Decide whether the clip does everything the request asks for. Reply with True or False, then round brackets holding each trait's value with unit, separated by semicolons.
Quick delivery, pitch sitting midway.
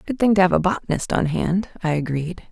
True (240 wpm; 180 Hz)